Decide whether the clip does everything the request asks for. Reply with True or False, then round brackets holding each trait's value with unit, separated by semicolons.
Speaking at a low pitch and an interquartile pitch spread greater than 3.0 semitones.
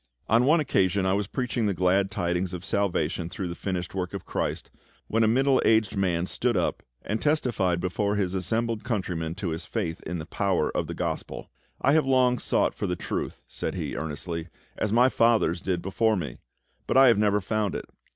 True (100 Hz; 4.2 semitones)